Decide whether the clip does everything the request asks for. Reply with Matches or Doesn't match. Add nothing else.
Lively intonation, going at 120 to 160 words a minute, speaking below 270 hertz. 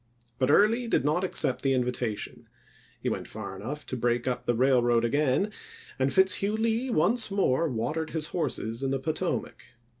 Doesn't match